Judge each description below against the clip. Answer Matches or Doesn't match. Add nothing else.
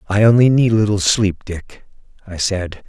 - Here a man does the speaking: Matches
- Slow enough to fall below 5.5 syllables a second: Matches